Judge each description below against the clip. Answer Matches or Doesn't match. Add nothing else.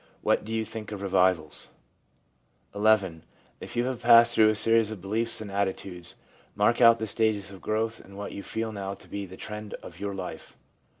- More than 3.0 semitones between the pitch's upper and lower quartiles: Doesn't match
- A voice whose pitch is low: Matches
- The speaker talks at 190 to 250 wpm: Matches